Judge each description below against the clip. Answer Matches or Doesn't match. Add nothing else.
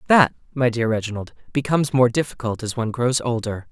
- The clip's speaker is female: Doesn't match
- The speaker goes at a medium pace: Matches